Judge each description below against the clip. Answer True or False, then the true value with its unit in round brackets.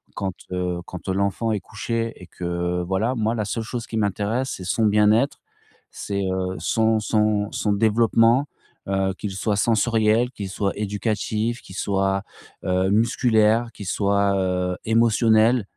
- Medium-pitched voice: False (105 Hz)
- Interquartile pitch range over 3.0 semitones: False (2.7 semitones)